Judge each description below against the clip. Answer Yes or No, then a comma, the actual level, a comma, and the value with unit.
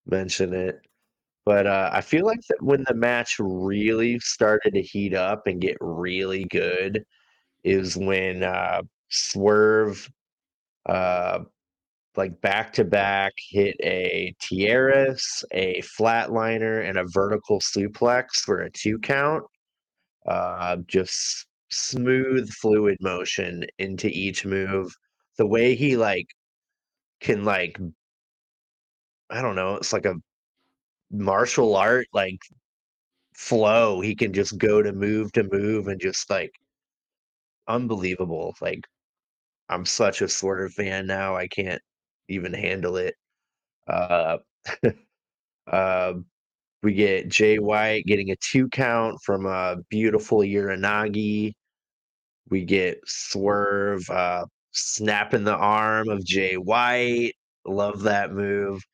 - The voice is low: Yes, low, 100 Hz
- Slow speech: Yes, slow, 120 wpm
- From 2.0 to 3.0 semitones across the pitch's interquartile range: Yes, narrow, 2.6 semitones